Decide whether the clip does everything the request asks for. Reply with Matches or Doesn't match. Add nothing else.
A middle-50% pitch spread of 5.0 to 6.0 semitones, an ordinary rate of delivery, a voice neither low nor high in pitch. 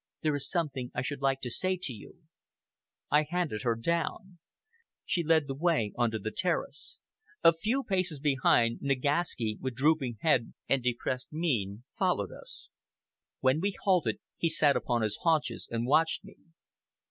Matches